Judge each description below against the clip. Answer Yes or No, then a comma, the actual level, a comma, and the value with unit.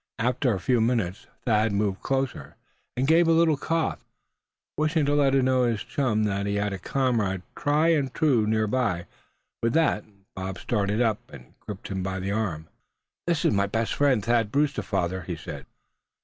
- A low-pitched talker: Yes, low, 115 Hz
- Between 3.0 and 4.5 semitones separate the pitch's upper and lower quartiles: No, wide, 5.4 semitones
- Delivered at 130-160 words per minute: No, average, 180 wpm